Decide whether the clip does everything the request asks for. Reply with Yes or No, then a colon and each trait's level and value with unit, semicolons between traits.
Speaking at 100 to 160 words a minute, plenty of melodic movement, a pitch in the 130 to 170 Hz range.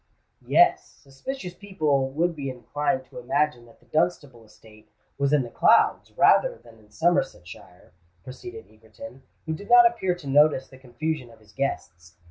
Yes: average, 155 wpm; wide, 6.7 semitones; medium, 140 Hz